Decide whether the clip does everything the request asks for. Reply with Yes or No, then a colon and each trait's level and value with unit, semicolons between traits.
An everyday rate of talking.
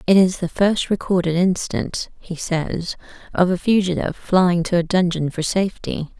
Yes: average, 165 wpm